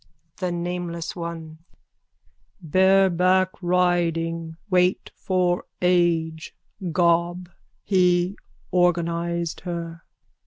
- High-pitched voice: No, medium, 175 Hz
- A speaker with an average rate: No, slow, 75 wpm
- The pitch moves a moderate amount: No, narrow, 1.3 semitones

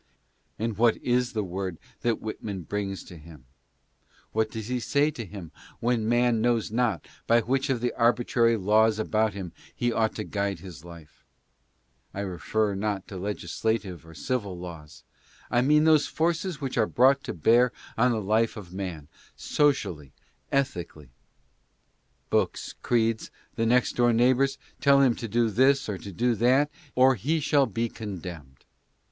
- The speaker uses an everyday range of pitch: Yes, average, 4.3 semitones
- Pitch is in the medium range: No, low, 110 Hz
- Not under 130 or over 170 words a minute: Yes, average, 160 wpm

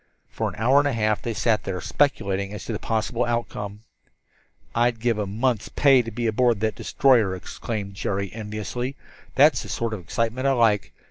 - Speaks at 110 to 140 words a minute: No, average, 190 wpm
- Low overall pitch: Yes, low, 115 Hz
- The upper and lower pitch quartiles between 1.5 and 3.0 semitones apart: Yes, average, 2.7 semitones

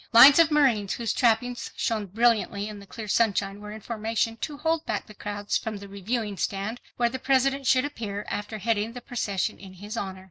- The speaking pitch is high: Yes, high, 220 Hz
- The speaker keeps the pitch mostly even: No, average, 3.2 semitones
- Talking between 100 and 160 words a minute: No, fast, 205 wpm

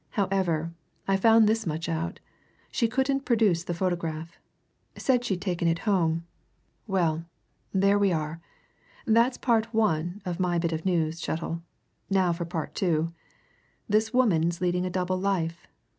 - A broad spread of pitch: No, average, 3.8 semitones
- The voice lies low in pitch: No, medium, 180 Hz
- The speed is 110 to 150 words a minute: Yes, average, 145 wpm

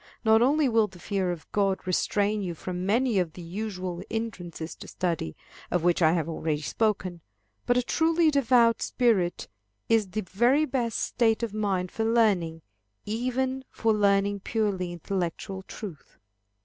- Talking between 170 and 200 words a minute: No, average, 155 wpm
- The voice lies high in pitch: Yes, high, 205 Hz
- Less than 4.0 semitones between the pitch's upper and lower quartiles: No, average, 4.4 semitones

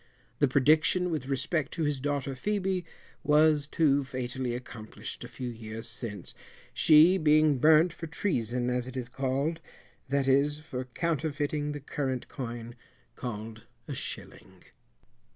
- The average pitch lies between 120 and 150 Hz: Yes, medium, 140 Hz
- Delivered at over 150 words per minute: No, slow, 135 wpm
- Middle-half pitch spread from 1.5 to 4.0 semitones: Yes, average, 3.7 semitones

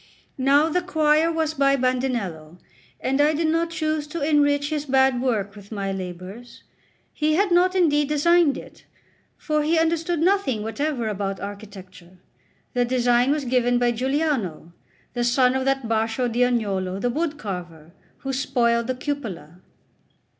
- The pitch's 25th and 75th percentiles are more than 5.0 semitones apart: Yes, wide, 5.6 semitones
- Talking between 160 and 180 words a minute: No, average, 150 wpm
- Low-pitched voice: No, very high, 260 Hz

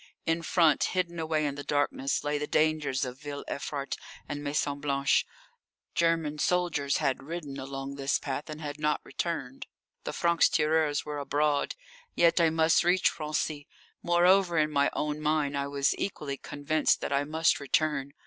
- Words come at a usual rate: Yes, average, 165 wpm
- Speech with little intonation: Yes, narrow, 2.2 semitones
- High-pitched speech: No, medium, 150 Hz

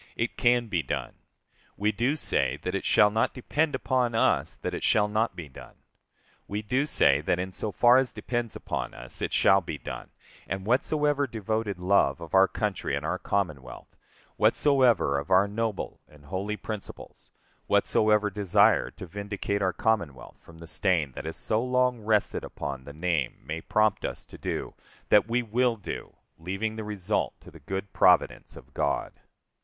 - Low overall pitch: Yes, low, 105 Hz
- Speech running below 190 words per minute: Yes, average, 175 wpm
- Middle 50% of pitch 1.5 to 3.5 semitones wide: No, average, 4.2 semitones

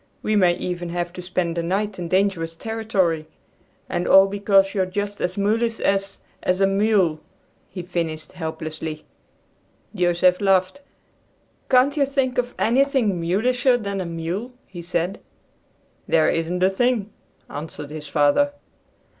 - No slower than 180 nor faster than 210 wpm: No, average, 140 wpm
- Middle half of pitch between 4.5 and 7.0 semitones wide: No, average, 3.8 semitones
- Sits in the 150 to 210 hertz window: Yes, high, 190 Hz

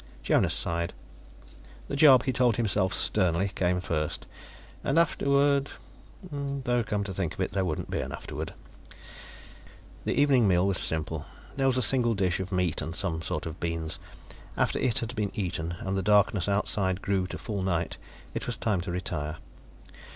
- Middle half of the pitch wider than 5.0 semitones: Yes, wide, 5.6 semitones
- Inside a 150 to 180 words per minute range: Yes, average, 175 wpm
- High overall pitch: No, very low, 95 Hz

